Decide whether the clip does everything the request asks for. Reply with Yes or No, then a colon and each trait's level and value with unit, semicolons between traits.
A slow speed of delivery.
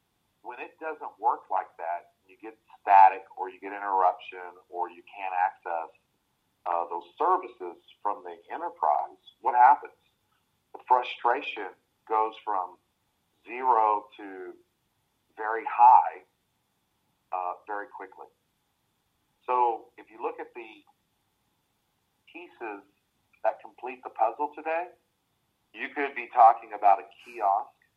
Yes: slow, 120 wpm